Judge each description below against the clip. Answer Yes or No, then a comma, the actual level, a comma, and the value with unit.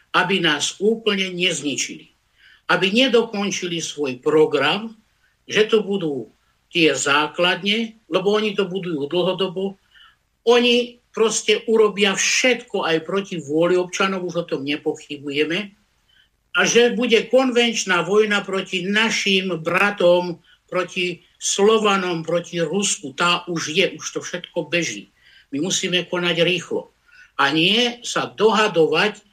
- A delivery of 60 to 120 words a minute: Yes, average, 115 wpm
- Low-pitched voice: No, high, 190 Hz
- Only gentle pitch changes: No, average, 3.9 semitones